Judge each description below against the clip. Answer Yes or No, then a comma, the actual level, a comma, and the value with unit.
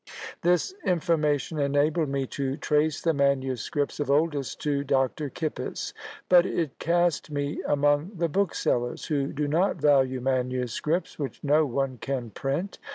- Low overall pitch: No, medium, 145 Hz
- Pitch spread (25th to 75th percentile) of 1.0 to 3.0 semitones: Yes, average, 2.7 semitones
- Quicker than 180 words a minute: No, average, 140 wpm